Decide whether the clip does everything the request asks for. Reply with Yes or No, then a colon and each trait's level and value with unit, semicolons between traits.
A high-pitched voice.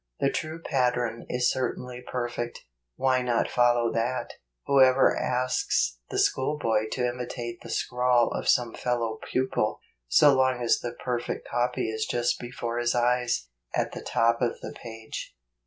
No: low, 120 Hz